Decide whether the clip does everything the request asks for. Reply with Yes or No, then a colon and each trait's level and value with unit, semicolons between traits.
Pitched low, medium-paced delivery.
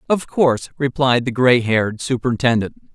Yes: low, 125 Hz; average, 145 wpm